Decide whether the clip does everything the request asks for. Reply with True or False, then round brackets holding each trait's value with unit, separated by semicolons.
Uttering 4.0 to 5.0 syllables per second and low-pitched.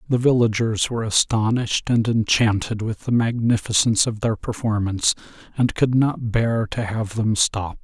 True (4.8 syllables/s; 110 Hz)